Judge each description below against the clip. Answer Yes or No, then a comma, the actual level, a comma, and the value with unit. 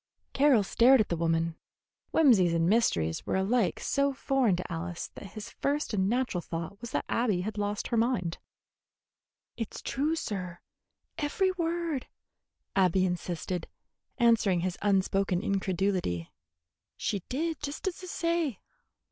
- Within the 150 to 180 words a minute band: No, average, 140 wpm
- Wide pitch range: Yes, wide, 6.9 semitones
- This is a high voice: Yes, high, 205 Hz